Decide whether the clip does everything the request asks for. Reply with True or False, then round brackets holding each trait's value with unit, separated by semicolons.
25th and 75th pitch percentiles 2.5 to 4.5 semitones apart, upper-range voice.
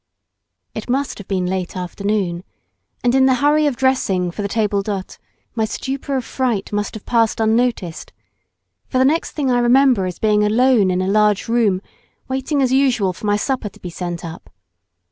False (5.1 semitones; 220 Hz)